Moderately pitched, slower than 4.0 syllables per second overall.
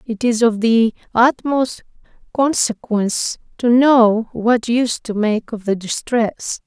No: high, 230 Hz; 3.7 syllables/s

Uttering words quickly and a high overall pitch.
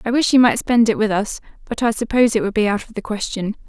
Yes: fast, 295 wpm; high, 220 Hz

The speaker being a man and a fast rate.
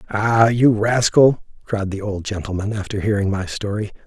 No: male; average, 160 wpm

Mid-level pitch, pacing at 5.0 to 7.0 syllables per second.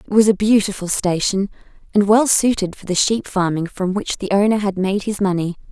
No: high, 200 Hz; 5.4 syllables/s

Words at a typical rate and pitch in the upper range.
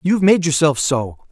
No: average, 180 wpm; medium, 155 Hz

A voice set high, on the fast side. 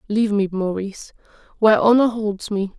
No: high, 210 Hz; average, 150 wpm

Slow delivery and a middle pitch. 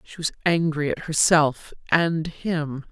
No: average, 145 wpm; medium, 155 Hz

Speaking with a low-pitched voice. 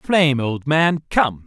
No: medium, 145 Hz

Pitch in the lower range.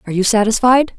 No: high, 225 Hz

